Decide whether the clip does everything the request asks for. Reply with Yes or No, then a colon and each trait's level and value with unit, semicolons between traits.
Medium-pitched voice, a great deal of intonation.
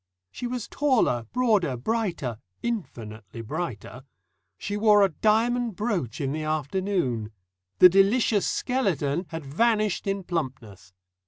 Yes: medium, 180 Hz; wide, 8.6 semitones